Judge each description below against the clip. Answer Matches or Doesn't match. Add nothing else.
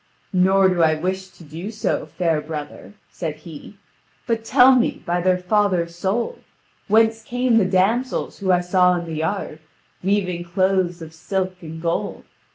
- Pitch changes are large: Doesn't match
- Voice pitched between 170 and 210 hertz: Matches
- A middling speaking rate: Matches